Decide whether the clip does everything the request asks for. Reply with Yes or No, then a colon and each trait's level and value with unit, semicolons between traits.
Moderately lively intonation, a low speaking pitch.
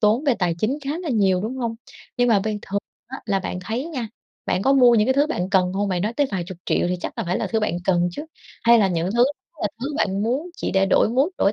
No: average, 4.9 semitones; high, 215 Hz